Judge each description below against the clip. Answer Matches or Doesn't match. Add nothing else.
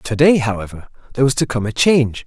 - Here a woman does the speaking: Doesn't match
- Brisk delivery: Matches